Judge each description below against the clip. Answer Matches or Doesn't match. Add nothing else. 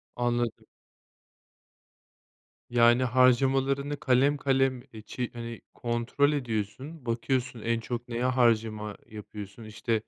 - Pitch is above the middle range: Doesn't match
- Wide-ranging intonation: Doesn't match